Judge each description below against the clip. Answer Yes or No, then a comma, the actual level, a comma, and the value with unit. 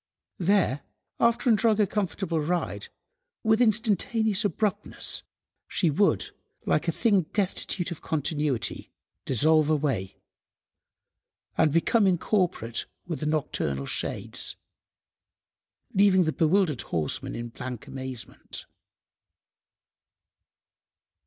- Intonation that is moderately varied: No, wide, 5.8 semitones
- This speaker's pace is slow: Yes, slow, 95 wpm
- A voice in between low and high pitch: Yes, medium, 170 Hz